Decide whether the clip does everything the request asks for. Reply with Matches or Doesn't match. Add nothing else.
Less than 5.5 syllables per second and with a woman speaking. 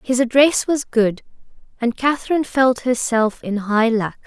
Matches